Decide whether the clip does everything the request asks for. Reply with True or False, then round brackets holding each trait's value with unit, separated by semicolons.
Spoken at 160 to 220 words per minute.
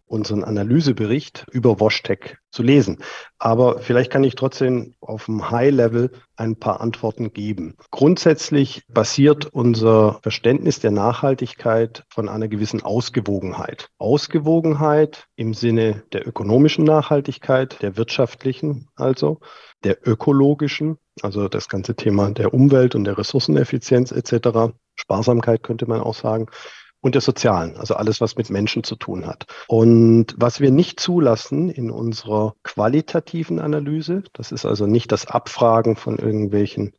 False (135 wpm)